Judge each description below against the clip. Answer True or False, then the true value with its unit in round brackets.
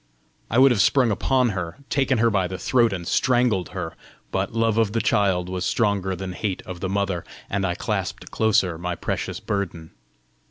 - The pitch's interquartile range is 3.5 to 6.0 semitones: True (3.9 semitones)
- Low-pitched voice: True (100 Hz)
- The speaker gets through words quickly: False (190 wpm)